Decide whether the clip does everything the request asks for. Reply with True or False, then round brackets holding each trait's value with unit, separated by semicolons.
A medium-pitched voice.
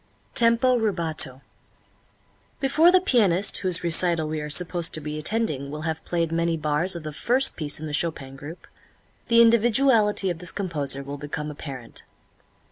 True (170 Hz)